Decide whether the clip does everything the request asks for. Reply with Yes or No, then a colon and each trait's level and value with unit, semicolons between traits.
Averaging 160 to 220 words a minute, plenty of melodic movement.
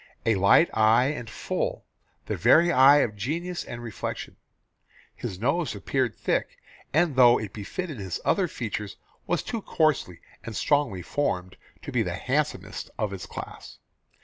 No: average, 150 wpm; wide, 6.7 semitones